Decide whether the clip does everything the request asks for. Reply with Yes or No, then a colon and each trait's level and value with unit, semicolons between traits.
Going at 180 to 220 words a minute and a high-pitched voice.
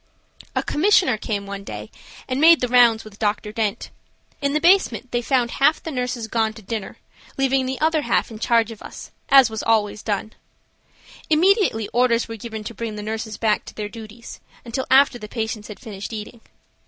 Yes: average, 190 wpm; high, 230 Hz